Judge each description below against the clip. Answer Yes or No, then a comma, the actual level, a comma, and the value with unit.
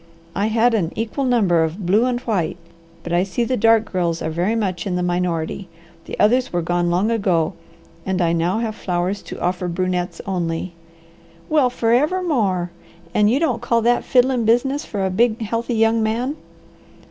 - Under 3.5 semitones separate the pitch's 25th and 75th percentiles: No, average, 4.9 semitones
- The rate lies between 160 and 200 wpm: Yes, average, 180 wpm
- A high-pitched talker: Yes, high, 205 Hz